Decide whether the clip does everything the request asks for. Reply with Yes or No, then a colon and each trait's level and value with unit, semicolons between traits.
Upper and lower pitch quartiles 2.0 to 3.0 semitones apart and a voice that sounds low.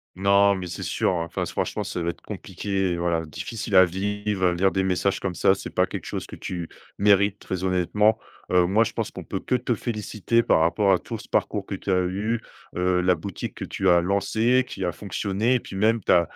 Yes: narrow, 2.6 semitones; very low, 95 Hz